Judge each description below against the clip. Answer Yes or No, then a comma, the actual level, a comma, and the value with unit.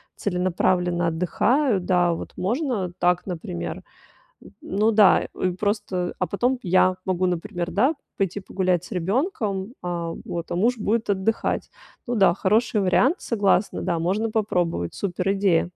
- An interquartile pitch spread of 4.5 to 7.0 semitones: No, average, 3.2 semitones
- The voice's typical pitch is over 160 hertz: Yes, high, 190 Hz